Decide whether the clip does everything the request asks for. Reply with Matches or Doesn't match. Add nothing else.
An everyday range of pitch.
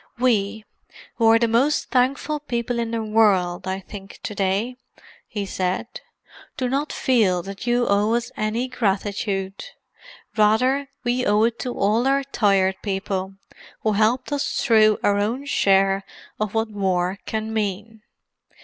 Matches